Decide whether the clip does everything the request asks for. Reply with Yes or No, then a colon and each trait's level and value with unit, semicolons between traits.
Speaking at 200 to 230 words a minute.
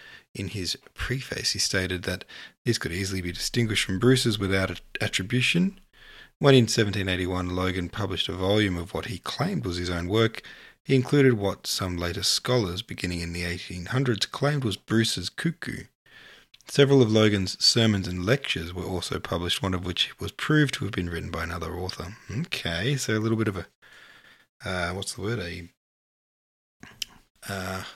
No: average, 165 wpm